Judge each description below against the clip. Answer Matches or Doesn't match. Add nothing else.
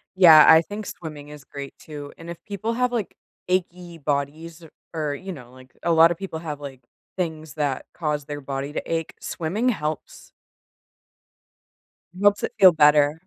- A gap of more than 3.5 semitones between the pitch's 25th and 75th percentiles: Doesn't match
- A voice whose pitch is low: Doesn't match